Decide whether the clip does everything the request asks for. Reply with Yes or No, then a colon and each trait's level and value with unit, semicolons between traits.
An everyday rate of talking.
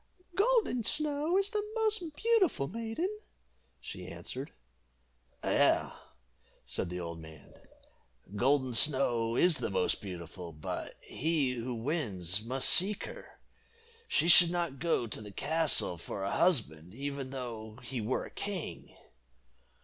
No: slow, 130 wpm